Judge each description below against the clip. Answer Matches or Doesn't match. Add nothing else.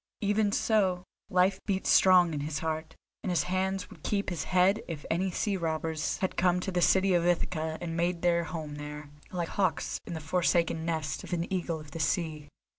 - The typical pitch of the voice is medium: Matches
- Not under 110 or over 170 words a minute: Doesn't match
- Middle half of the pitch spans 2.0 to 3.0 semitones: Matches